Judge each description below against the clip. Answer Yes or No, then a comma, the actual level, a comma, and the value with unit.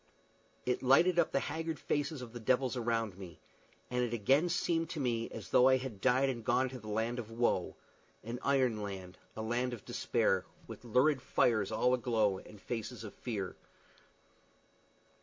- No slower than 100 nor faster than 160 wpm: No, average, 175 wpm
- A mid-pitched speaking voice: No, low, 120 Hz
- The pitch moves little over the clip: No, average, 3.0 semitones